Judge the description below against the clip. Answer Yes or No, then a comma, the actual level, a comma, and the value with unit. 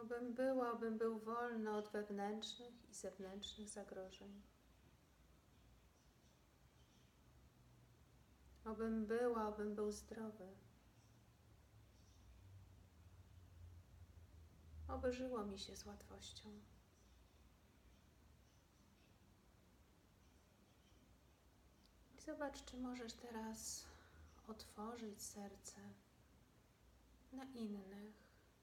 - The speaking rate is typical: No, slow, 65 wpm